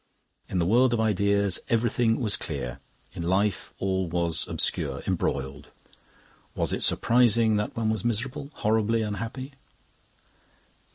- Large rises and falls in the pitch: No, average, 3.9 semitones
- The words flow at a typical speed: No, slow, 125 wpm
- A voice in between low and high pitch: No, low, 105 Hz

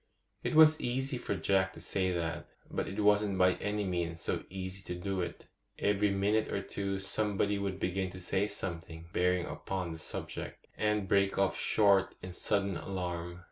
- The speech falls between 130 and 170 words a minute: No, average, 180 wpm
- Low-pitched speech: Yes, very low, 95 Hz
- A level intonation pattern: Yes, narrow, 2.0 semitones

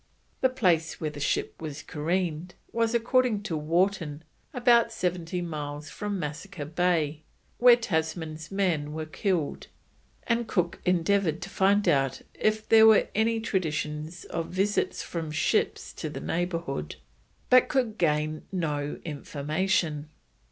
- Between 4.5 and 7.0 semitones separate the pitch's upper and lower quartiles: Yes, average, 4.8 semitones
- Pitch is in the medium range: Yes, medium, 170 Hz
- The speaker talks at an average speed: No, slow, 130 wpm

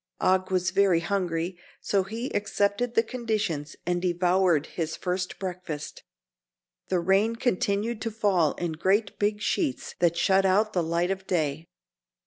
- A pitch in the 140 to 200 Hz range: Yes, high, 190 Hz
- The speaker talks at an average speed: Yes, average, 145 wpm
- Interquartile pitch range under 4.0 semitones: Yes, average, 2.9 semitones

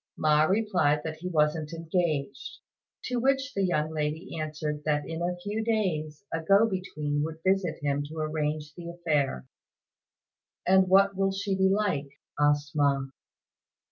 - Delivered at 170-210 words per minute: No, average, 150 wpm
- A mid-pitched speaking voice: Yes, medium, 160 Hz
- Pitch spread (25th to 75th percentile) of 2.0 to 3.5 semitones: No, average, 4.1 semitones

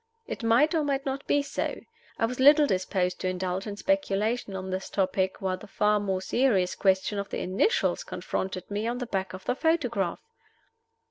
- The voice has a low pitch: No, high, 205 Hz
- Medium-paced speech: Yes, average, 190 wpm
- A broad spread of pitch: Yes, wide, 5.9 semitones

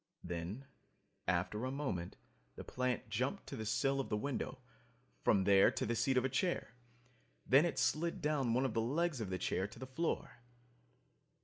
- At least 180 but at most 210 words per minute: Yes, average, 185 wpm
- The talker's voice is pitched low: Yes, low, 125 Hz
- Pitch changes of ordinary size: Yes, average, 4.7 semitones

